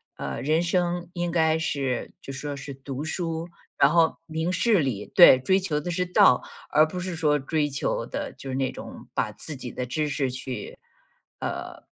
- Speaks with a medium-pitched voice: Yes, medium, 155 Hz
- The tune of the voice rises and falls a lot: No, average, 4.2 semitones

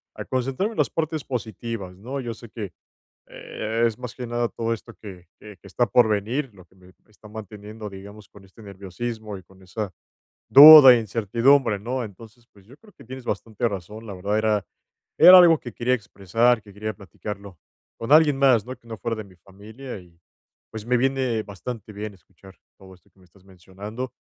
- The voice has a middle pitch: No, low, 110 Hz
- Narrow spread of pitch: No, average, 3.7 semitones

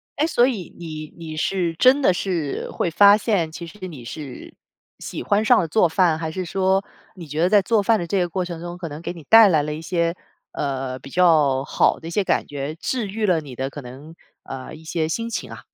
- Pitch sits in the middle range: Yes, medium, 170 Hz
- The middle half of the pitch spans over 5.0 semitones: No, average, 3.9 semitones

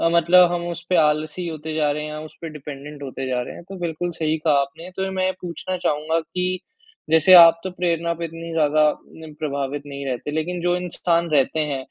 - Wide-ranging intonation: No, narrow, 2.5 semitones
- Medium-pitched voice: Yes, medium, 160 Hz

